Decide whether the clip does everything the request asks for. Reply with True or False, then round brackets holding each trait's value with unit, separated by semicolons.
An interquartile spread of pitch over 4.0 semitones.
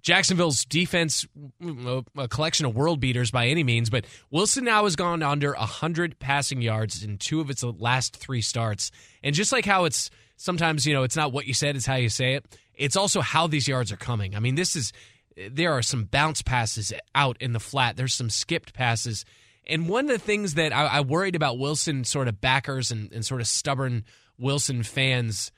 True (5.1 semitones)